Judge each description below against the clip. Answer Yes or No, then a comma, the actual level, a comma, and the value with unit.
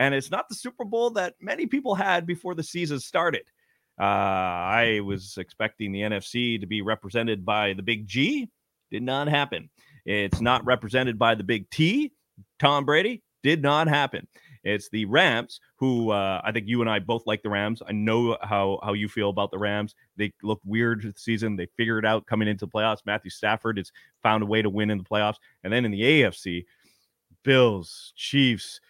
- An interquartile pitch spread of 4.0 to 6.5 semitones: Yes, average, 4.8 semitones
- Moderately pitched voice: No, low, 110 Hz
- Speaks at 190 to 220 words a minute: Yes, average, 200 wpm